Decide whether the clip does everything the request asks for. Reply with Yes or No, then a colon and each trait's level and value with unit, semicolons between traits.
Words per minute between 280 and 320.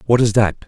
No: fast, 265 wpm